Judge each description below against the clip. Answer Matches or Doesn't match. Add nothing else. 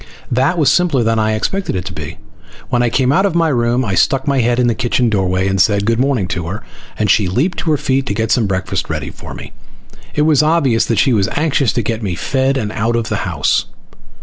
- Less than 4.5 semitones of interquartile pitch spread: Doesn't match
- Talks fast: Matches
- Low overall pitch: Matches